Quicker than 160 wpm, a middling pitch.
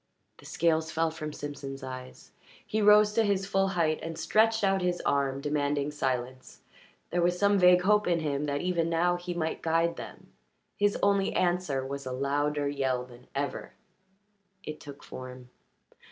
Yes: average, 170 wpm; medium, 160 Hz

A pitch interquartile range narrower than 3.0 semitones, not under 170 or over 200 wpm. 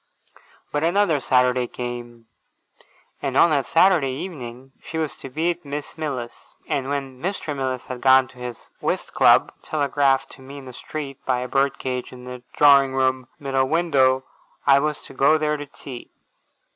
Yes: narrow, 2.5 semitones; average, 175 wpm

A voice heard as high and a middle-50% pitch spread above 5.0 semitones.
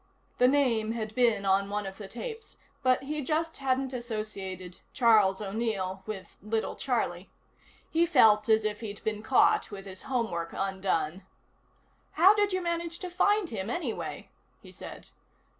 Yes: high, 220 Hz; wide, 5.5 semitones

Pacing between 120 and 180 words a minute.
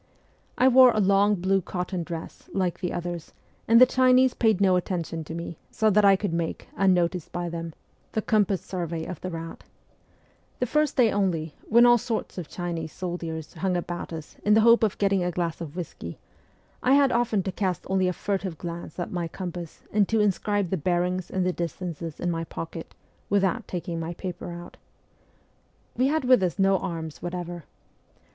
No: average, 190 wpm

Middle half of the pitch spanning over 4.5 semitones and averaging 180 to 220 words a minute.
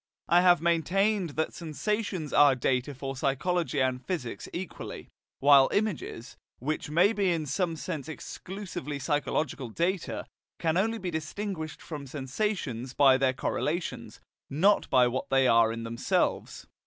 No: average, 5.2 semitones; average, 140 wpm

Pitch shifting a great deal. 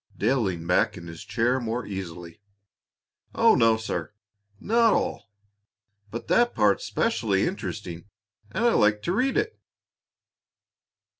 Yes: wide, 5.9 semitones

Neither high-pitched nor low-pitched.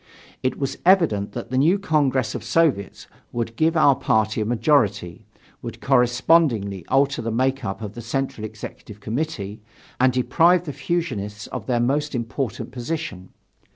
No: low, 125 Hz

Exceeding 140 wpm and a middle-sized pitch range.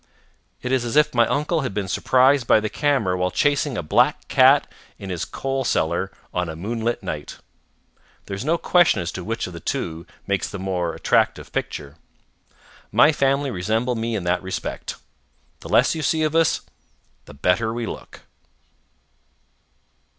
No: average, 170 wpm; wide, 7.0 semitones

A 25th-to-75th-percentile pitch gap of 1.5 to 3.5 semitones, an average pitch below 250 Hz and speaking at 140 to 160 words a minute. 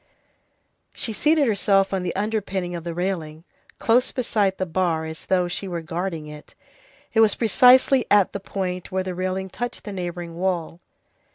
No: average, 3.0 semitones; medium, 185 Hz; average, 170 wpm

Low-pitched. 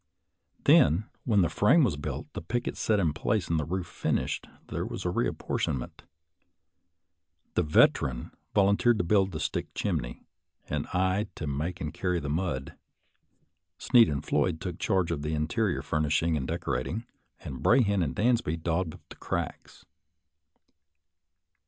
Yes: very low, 85 Hz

